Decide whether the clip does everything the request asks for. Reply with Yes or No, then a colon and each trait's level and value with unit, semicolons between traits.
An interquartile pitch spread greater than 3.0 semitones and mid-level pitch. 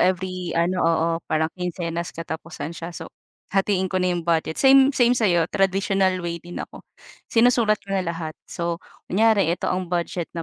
No: narrow, 2.6 semitones; medium, 180 Hz